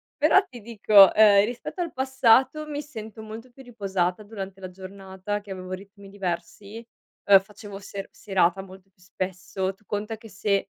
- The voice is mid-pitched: No, high, 205 Hz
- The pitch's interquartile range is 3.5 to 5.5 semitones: No, average, 2.7 semitones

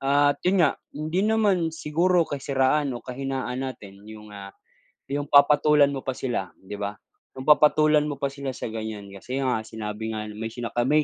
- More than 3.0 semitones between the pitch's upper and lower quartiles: Yes, average, 5.2 semitones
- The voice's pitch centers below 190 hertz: Yes, low, 135 Hz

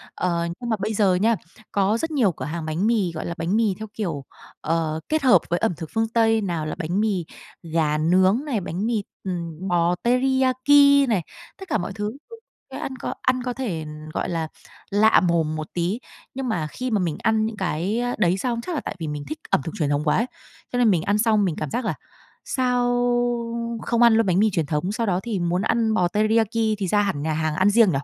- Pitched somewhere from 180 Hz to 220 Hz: Yes, high, 200 Hz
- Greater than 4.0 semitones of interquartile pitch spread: Yes, average, 5.2 semitones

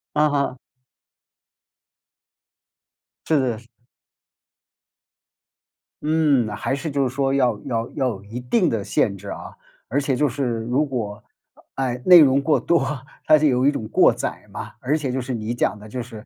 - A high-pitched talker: No, low, 130 Hz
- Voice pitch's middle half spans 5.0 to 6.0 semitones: No, average, 3.8 semitones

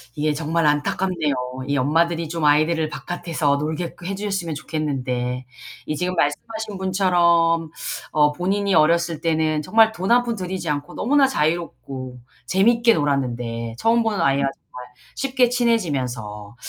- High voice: No, medium, 165 Hz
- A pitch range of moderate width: Yes, average, 4.6 semitones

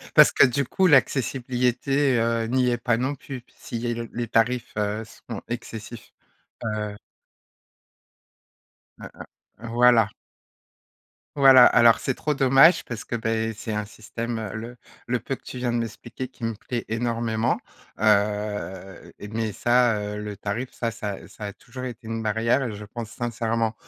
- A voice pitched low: Yes, low, 115 Hz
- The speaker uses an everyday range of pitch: No, narrow, 2.2 semitones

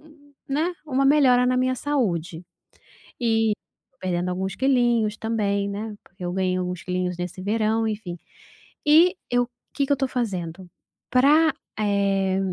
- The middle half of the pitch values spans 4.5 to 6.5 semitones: Yes, wide, 5.5 semitones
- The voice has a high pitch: Yes, high, 220 Hz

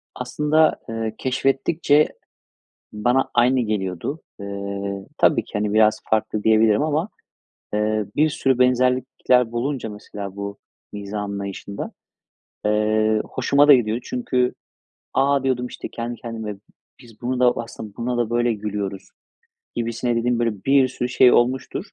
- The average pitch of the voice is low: Yes, low, 115 Hz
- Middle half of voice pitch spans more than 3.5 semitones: No, average, 3.2 semitones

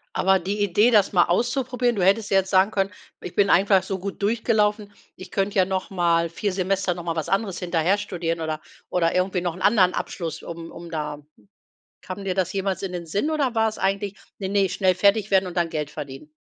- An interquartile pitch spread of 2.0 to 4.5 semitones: Yes, average, 2.8 semitones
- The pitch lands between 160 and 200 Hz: Yes, high, 190 Hz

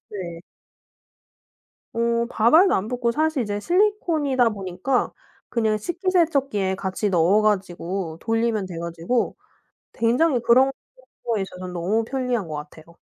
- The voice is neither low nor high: No, high, 225 Hz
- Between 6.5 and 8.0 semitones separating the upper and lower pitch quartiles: No, wide, 5.6 semitones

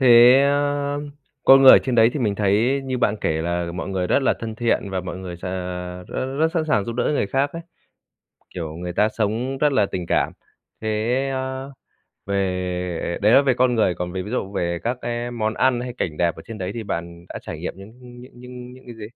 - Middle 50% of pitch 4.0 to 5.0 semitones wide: No, wide, 5.6 semitones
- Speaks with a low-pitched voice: Yes, low, 115 Hz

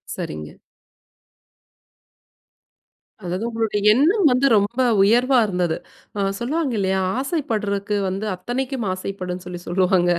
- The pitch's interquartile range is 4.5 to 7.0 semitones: Yes, average, 5.3 semitones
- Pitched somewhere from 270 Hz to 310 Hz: No, high, 205 Hz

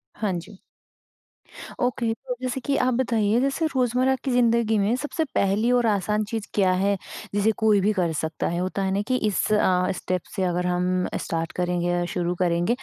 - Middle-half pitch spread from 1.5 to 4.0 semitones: No, average, 4.8 semitones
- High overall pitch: Yes, high, 205 Hz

